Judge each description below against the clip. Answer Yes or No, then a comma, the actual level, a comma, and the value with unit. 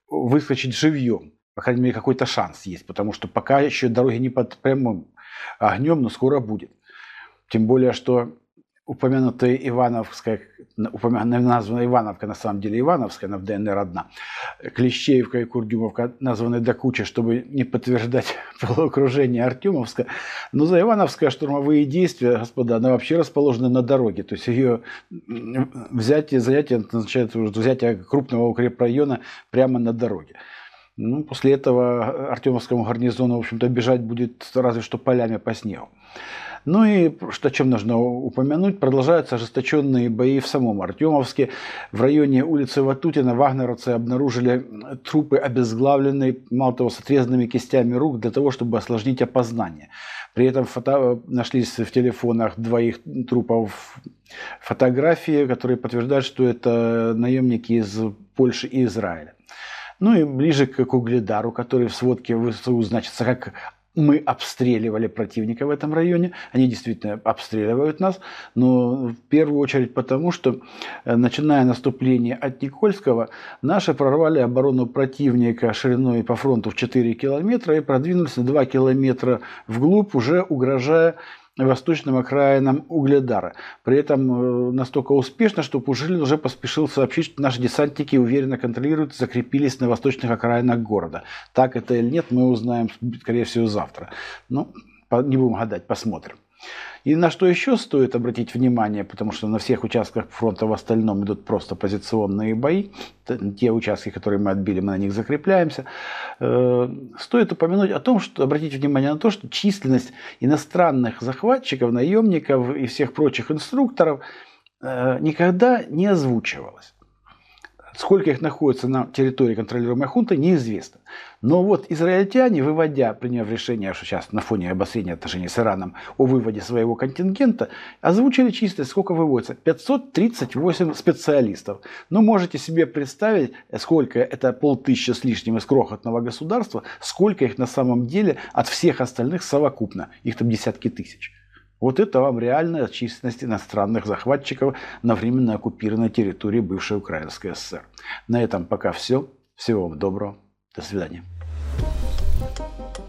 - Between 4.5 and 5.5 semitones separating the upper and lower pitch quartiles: No, average, 3.3 semitones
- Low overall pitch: Yes, low, 125 Hz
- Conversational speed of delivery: Yes, average, 140 wpm